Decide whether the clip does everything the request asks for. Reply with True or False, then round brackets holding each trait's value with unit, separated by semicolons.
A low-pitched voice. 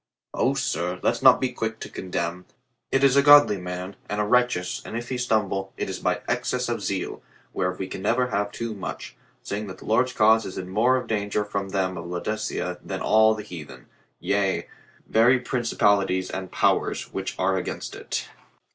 True (105 Hz)